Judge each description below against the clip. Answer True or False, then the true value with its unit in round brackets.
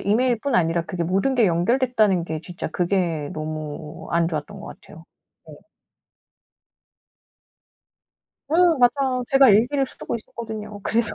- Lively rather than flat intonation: True (6.8 semitones)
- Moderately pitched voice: False (205 Hz)